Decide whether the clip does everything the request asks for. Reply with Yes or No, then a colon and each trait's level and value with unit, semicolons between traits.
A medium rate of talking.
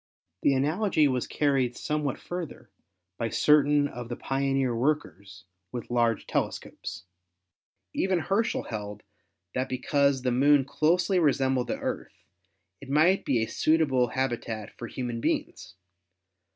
No: slow, 125 wpm